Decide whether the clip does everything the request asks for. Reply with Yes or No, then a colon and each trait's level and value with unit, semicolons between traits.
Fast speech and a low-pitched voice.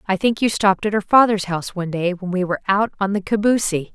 No: fast, 260 wpm; high, 195 Hz